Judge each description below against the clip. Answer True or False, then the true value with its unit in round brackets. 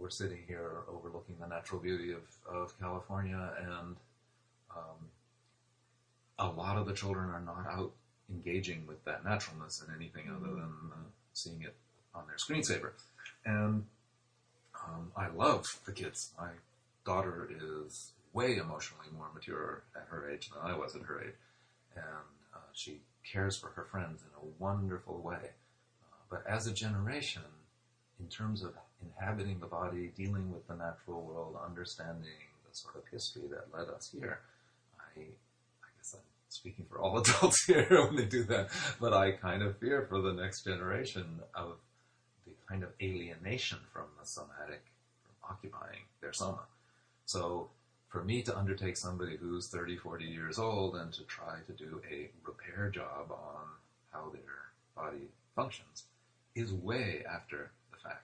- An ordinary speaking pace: True (160 wpm)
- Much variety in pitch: False (4.2 semitones)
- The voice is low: True (95 Hz)